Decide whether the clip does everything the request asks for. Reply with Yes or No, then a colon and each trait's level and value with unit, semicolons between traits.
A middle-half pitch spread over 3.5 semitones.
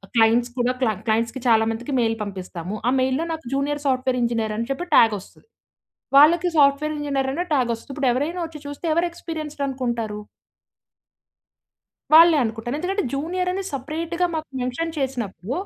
Yes: average, 5.0 semitones